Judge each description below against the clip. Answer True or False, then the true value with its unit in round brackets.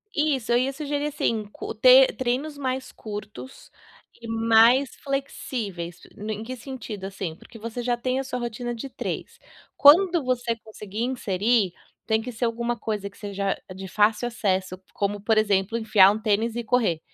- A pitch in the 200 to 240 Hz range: True (230 Hz)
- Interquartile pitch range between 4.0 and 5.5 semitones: False (3.5 semitones)